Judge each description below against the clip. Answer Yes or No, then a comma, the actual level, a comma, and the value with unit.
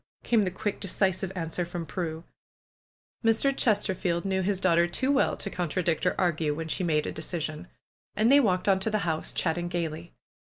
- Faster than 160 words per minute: Yes, average, 185 wpm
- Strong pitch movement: No, average, 3.0 semitones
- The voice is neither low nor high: Yes, medium, 180 Hz